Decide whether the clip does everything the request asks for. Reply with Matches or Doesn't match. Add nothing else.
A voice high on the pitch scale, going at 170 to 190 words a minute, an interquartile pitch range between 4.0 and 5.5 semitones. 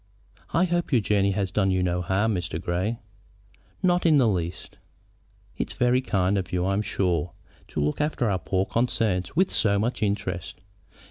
Doesn't match